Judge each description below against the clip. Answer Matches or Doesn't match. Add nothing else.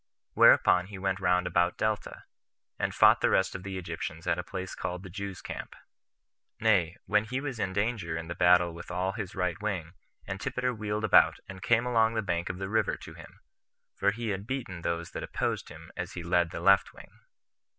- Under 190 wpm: Doesn't match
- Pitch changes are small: Doesn't match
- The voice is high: Doesn't match